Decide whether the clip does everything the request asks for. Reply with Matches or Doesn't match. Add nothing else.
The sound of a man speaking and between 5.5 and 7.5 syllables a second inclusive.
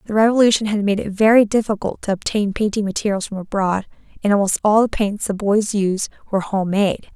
Doesn't match